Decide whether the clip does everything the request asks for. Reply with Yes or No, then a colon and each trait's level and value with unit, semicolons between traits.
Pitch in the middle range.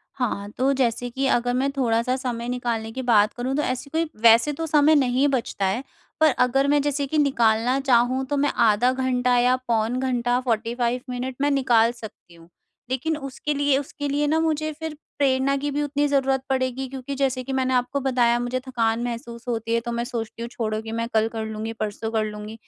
No: very high, 250 Hz